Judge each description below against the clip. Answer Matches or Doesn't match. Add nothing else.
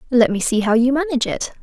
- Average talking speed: Doesn't match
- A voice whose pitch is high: Matches